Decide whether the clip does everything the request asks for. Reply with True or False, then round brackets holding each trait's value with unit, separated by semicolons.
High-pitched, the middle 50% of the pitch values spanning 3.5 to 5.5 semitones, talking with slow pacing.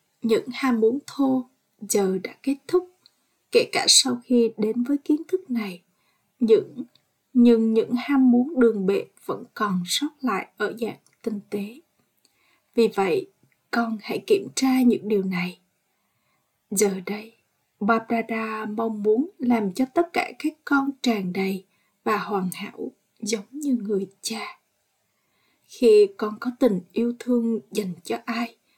True (230 Hz; 4.2 semitones; 150 wpm)